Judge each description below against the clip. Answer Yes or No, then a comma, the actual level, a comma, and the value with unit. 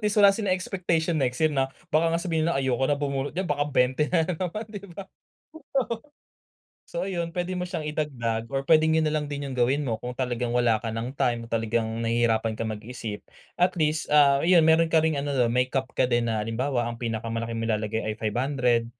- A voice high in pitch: No, medium, 140 Hz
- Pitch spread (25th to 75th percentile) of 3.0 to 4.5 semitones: No, wide, 5.6 semitones